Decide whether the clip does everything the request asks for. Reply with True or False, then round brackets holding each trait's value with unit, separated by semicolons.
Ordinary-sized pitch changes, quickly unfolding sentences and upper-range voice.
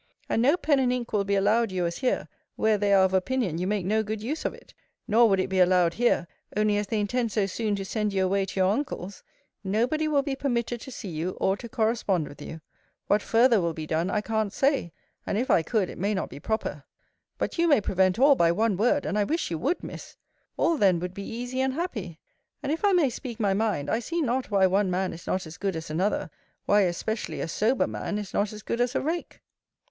True (4.4 semitones; 250 wpm; 210 Hz)